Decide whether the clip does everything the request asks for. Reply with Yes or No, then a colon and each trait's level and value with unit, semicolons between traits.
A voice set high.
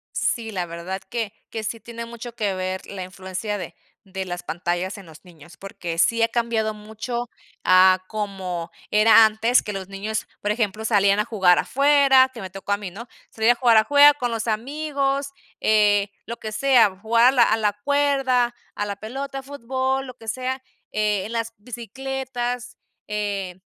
Yes: high, 220 Hz